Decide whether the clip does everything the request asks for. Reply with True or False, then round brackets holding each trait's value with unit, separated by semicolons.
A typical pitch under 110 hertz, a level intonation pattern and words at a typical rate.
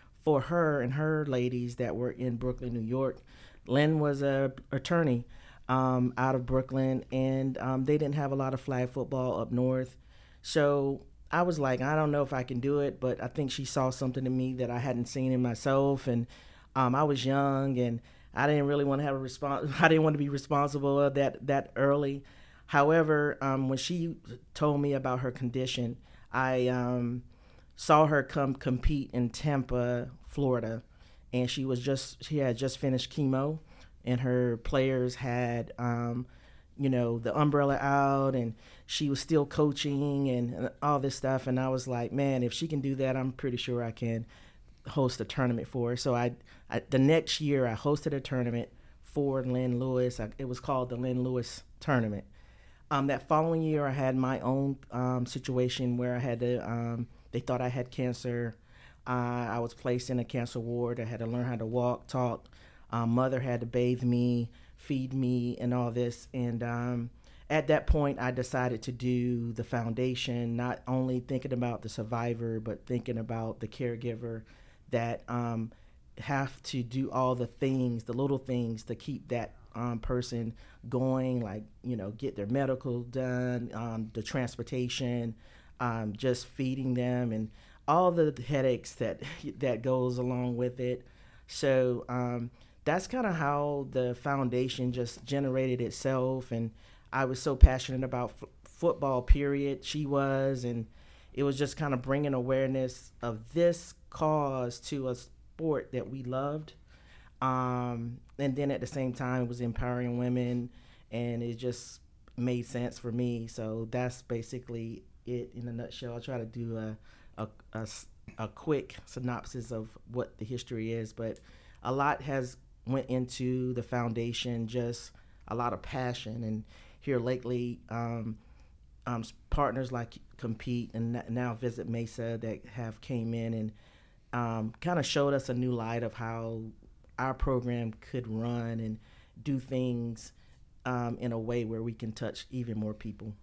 False (125 Hz; 2.1 semitones; 175 wpm)